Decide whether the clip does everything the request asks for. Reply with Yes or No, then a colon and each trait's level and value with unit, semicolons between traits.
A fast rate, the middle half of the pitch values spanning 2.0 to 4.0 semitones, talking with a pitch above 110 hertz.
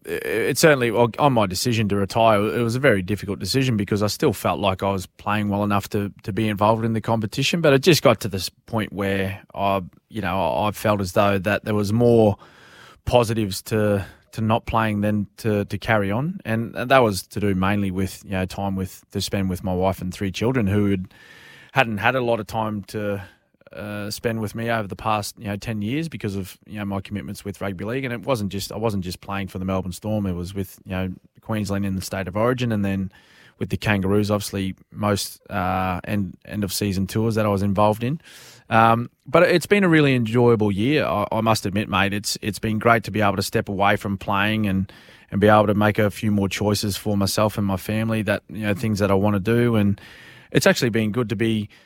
No: fast, 235 wpm; narrow, 2.4 semitones; low, 105 Hz